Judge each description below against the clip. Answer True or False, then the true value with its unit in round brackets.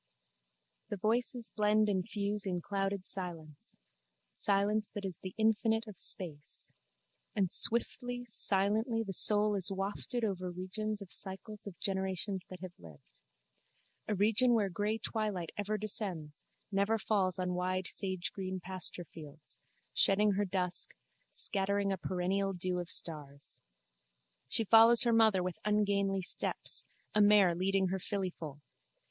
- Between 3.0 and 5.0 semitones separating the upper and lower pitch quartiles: False (2.5 semitones)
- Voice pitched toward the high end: True (195 Hz)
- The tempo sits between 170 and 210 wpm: False (135 wpm)